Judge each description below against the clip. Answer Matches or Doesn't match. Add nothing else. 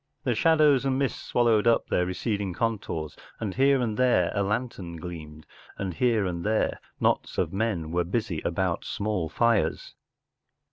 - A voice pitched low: Matches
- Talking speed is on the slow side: Doesn't match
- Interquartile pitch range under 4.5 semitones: Doesn't match